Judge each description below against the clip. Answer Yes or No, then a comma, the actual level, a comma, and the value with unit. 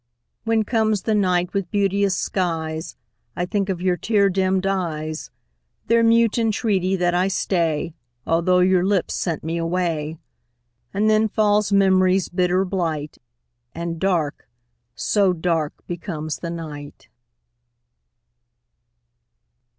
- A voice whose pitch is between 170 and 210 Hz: Yes, medium, 185 Hz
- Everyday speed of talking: No, slow, 120 wpm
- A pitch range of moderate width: Yes, average, 3.1 semitones